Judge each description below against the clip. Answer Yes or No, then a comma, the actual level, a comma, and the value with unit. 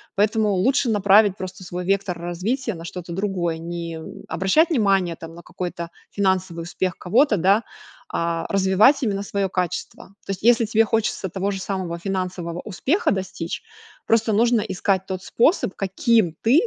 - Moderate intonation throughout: Yes, average, 3.4 semitones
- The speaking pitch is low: No, high, 190 Hz